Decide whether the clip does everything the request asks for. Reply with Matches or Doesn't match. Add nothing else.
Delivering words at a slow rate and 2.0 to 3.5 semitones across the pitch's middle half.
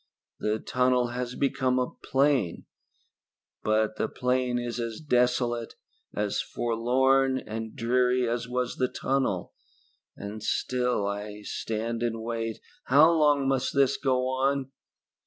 Matches